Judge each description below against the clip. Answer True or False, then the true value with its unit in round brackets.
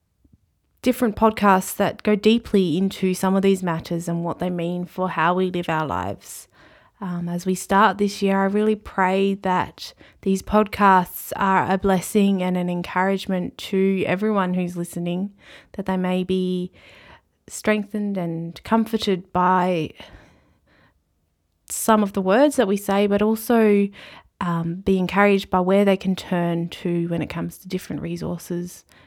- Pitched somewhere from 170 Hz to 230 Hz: True (185 Hz)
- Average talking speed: True (155 wpm)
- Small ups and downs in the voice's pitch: True (2.3 semitones)